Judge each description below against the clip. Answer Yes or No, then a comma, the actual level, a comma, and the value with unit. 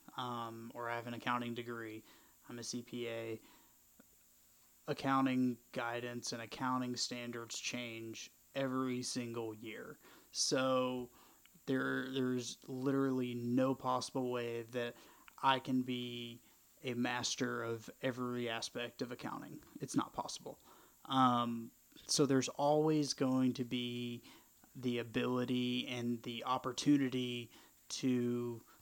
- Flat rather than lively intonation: Yes, narrow, 1.5 semitones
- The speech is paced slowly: Yes, slow, 110 wpm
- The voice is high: No, low, 120 Hz